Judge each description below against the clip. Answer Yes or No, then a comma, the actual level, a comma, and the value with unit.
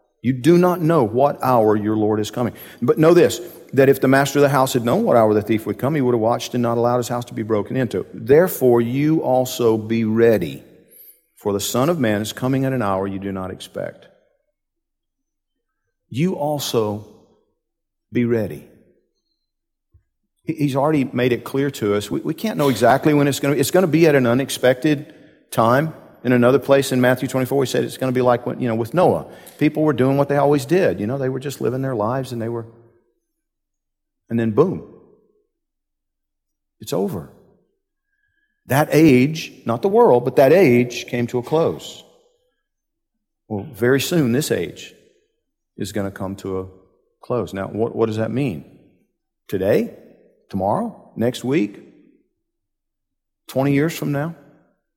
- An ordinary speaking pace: Yes, average, 180 wpm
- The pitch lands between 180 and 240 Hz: No, low, 130 Hz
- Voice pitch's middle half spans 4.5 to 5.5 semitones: Yes, average, 4.9 semitones